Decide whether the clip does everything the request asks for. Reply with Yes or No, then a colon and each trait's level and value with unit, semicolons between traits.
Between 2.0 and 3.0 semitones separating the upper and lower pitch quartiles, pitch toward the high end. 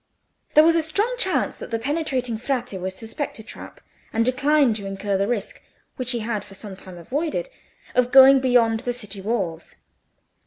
No: average, 4.9 semitones; high, 240 Hz